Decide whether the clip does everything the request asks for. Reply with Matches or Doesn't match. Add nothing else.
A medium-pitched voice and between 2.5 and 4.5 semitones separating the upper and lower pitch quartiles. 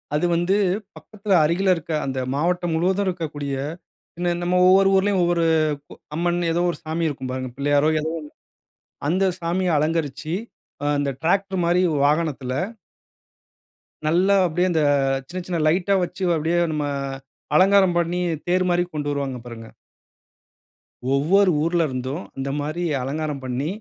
Matches